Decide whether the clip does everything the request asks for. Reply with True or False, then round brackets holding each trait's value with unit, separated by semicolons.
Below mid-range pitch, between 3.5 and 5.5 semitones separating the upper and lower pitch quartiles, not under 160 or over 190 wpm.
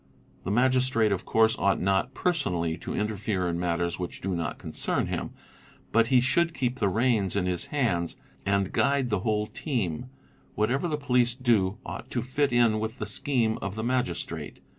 True (110 Hz; 5.1 semitones; 180 wpm)